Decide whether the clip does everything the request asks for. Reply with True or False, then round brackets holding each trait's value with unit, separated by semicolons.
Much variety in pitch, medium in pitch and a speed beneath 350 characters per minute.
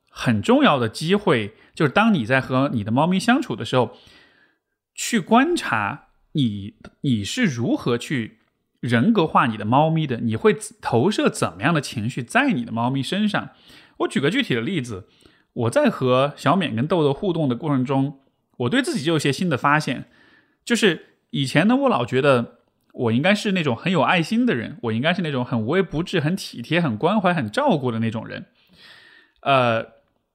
True (7.8 semitones; 145 Hz; 265 characters per minute)